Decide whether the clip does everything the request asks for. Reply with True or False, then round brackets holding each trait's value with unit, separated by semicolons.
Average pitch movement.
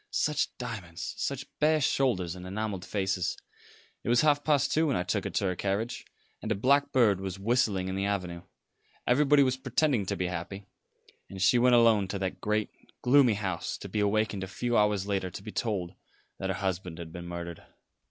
True (4.8 semitones)